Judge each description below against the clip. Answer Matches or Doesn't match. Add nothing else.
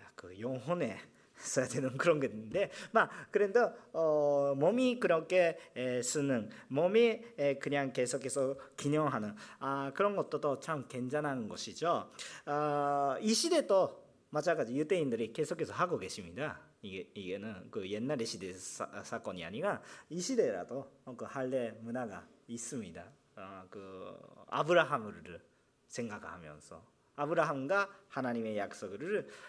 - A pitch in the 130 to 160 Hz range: Matches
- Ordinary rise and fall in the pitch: Matches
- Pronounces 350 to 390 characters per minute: Doesn't match